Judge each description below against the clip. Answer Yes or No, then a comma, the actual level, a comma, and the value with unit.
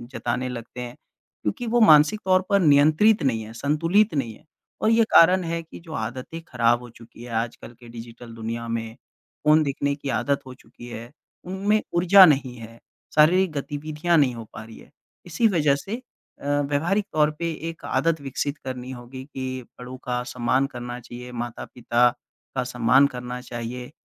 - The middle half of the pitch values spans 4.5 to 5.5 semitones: Yes, average, 5.1 semitones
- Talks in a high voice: No, low, 135 Hz